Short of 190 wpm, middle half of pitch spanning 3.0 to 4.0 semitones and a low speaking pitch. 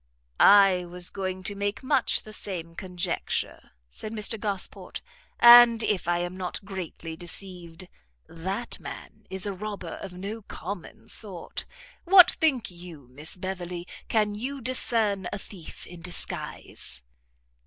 No: slow, 135 wpm; average, 3.3 semitones; high, 190 Hz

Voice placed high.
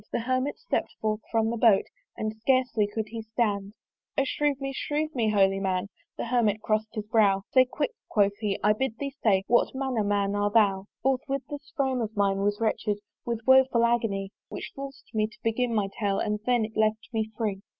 Yes: high, 220 Hz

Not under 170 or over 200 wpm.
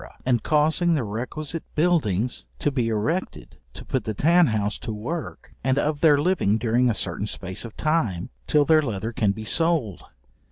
Yes: average, 175 wpm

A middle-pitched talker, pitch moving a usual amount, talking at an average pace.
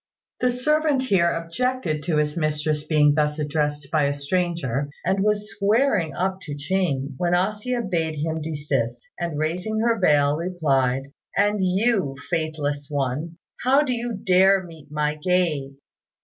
Yes: medium, 165 Hz; average, 4.9 semitones; average, 150 wpm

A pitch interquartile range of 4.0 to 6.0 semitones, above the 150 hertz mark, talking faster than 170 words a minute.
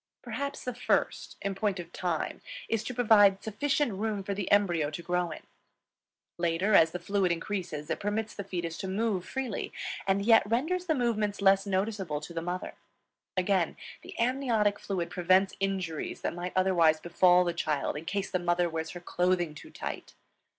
No: average, 3.3 semitones; high, 190 Hz; average, 180 wpm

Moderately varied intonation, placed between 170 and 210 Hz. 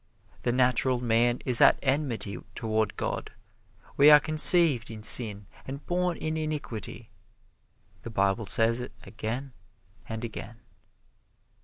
No: average, 4.1 semitones; low, 120 Hz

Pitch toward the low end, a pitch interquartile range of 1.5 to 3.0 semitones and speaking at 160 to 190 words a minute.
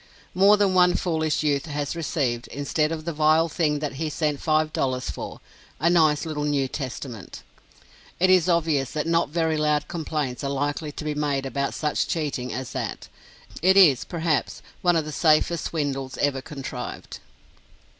No: medium, 150 Hz; average, 2.7 semitones; average, 170 wpm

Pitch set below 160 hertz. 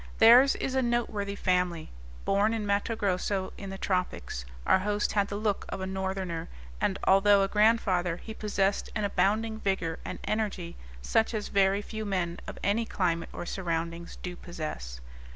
No: high, 195 Hz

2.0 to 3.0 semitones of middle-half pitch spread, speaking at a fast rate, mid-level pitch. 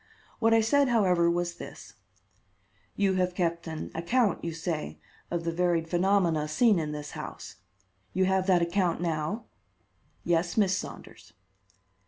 No: average, 2.7 semitones; average, 145 wpm; medium, 175 Hz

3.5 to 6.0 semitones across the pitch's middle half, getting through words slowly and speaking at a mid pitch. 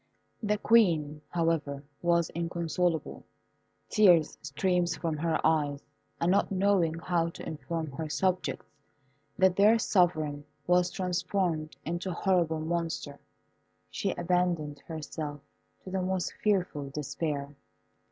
No: average, 2.9 semitones; slow, 115 wpm; medium, 170 Hz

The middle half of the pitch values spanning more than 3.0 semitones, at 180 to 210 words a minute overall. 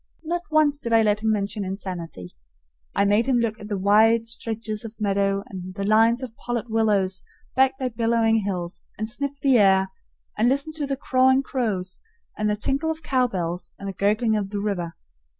Yes: average, 3.8 semitones; average, 190 wpm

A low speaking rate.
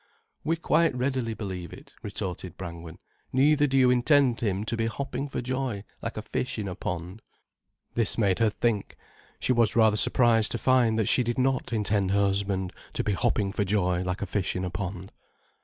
No: average, 195 wpm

